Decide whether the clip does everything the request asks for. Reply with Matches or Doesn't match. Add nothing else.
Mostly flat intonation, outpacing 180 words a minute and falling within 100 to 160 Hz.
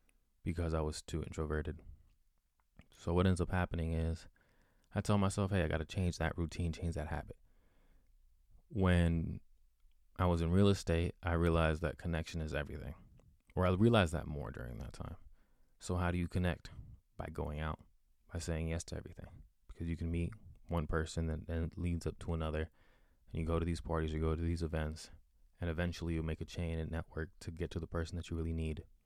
Doesn't match